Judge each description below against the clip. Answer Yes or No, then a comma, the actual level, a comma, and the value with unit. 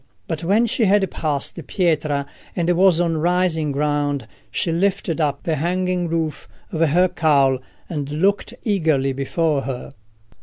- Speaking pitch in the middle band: Yes, medium, 165 Hz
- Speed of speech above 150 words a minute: No, average, 145 wpm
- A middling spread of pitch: Yes, average, 3.8 semitones